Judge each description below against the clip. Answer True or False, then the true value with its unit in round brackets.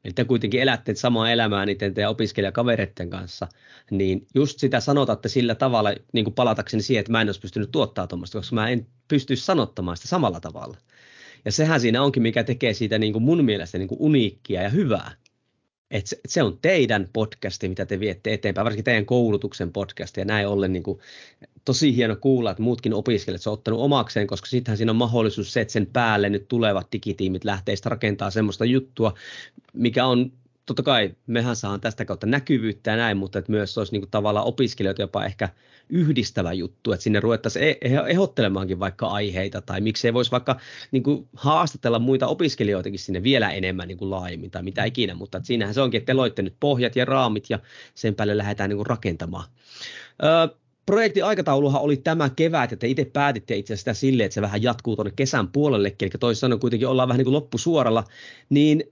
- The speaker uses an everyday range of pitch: True (4.3 semitones)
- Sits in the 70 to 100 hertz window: False (115 Hz)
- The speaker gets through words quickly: True (190 wpm)